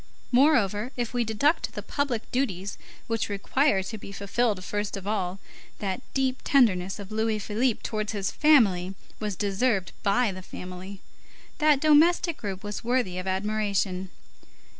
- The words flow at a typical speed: Yes, average, 145 wpm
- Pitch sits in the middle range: No, high, 210 Hz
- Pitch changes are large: No, average, 4.3 semitones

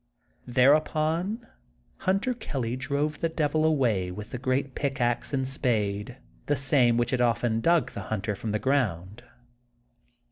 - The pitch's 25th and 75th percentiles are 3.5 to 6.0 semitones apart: Yes, average, 4.6 semitones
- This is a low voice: Yes, low, 130 Hz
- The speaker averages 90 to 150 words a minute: Yes, average, 140 wpm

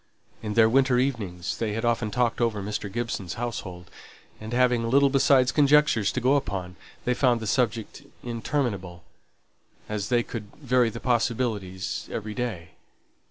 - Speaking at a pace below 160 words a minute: Yes, average, 150 wpm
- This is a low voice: Yes, low, 115 Hz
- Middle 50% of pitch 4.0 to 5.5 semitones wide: No, average, 3.2 semitones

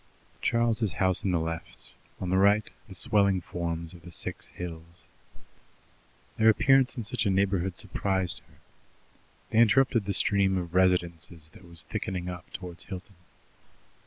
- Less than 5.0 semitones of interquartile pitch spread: Yes, average, 2.9 semitones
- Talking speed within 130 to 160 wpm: Yes, average, 150 wpm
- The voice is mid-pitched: No, very low, 95 Hz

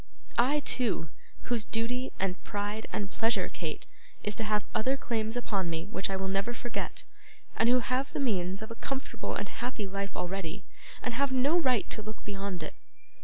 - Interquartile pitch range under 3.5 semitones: No, average, 4.0 semitones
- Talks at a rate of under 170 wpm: No, average, 190 wpm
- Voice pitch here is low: No, high, 220 Hz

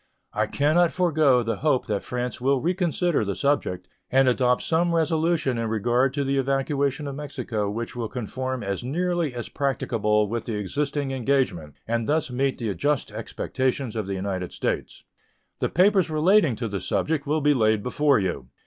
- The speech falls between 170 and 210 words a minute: Yes, average, 175 wpm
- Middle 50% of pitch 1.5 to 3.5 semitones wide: No, average, 4.8 semitones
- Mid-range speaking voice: No, low, 130 Hz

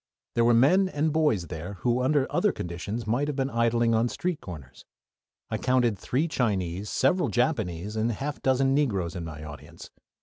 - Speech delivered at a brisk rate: No, average, 180 wpm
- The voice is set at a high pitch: No, low, 115 Hz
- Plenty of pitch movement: Yes, wide, 6.5 semitones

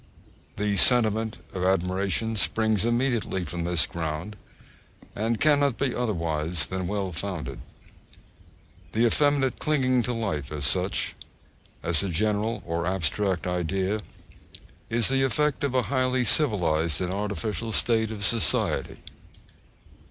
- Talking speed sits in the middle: No, slow, 120 wpm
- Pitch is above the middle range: No, low, 105 Hz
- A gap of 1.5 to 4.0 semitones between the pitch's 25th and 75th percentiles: No, average, 4.9 semitones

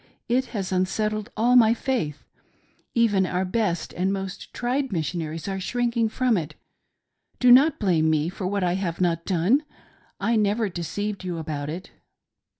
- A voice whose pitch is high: Yes, high, 195 Hz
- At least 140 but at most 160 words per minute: Yes, average, 155 wpm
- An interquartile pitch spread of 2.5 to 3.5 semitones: No, average, 4.9 semitones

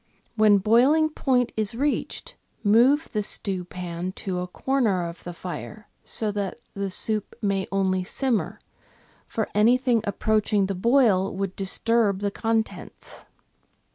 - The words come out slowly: Yes, slow, 130 wpm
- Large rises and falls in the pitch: No, average, 3.5 semitones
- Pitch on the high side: Yes, high, 210 Hz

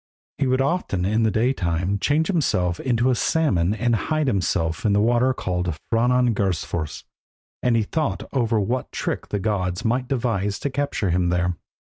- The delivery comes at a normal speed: Yes, average, 165 wpm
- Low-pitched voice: Yes, low, 110 Hz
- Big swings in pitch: Yes, wide, 5.9 semitones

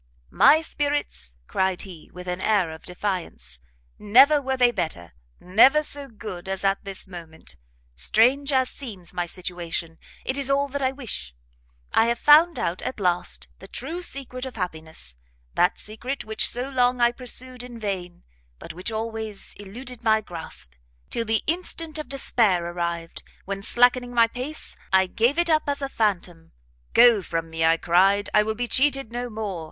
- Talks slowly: No, average, 170 wpm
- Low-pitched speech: No, high, 220 Hz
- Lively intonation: Yes, wide, 6.4 semitones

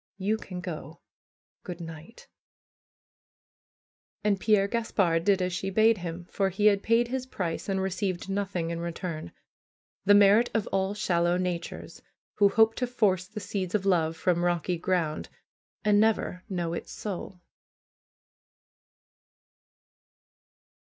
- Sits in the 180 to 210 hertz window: Yes, high, 190 Hz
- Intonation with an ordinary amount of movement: Yes, average, 3.1 semitones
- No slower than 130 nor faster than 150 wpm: Yes, slow, 135 wpm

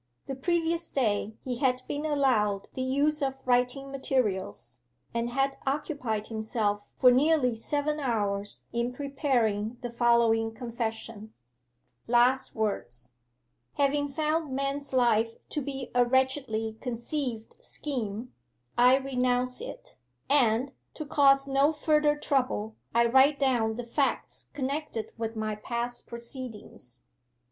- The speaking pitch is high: Yes, very high, 250 Hz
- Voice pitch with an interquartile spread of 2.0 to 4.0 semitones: Yes, average, 3.6 semitones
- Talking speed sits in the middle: No, slow, 120 wpm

